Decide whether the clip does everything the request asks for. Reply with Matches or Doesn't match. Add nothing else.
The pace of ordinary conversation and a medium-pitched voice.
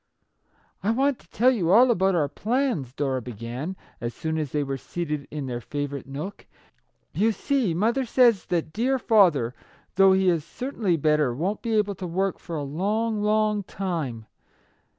Matches